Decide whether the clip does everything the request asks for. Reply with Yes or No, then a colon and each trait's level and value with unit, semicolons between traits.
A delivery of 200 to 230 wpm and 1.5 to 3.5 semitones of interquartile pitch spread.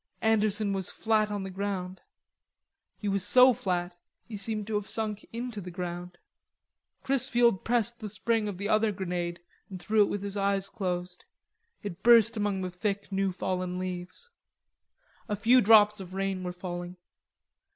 No: average, 160 wpm; average, 2.9 semitones